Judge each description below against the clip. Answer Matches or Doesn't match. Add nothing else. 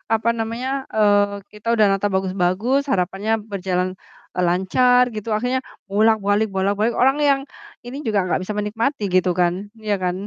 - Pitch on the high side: Matches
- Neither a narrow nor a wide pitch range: Matches